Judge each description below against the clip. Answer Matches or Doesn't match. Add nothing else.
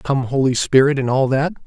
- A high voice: Doesn't match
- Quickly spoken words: Matches